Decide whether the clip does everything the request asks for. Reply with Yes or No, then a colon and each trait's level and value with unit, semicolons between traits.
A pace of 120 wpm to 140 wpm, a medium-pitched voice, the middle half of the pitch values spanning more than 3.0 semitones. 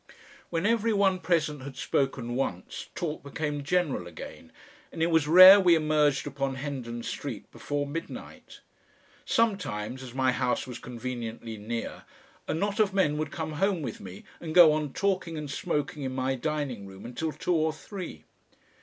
No: average, 165 wpm; medium, 150 Hz; average, 4.6 semitones